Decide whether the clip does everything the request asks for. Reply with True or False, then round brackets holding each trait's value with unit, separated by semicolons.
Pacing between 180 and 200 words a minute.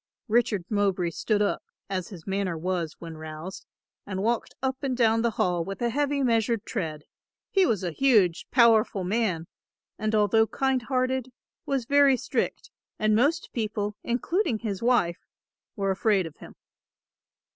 False (155 wpm)